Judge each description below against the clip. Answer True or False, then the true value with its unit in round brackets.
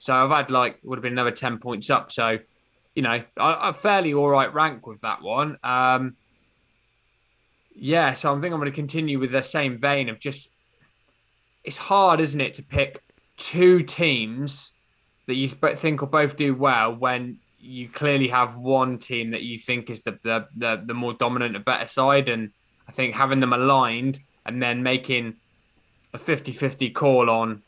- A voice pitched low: True (130 Hz)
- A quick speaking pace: False (180 wpm)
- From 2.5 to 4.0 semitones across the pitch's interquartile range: True (3.1 semitones)